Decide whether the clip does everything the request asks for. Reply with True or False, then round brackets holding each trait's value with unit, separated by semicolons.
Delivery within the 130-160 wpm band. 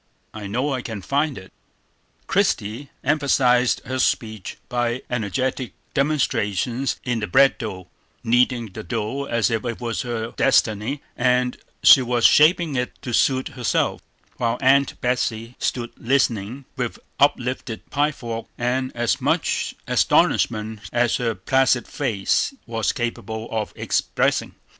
True (135 wpm)